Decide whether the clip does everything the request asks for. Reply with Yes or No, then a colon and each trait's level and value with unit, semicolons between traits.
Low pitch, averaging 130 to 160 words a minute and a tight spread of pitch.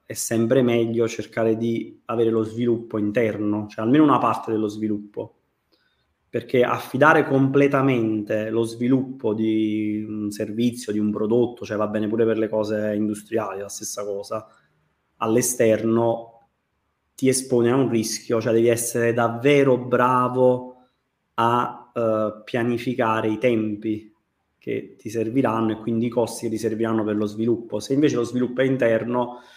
Yes: low, 115 Hz; average, 145 wpm; narrow, 2.2 semitones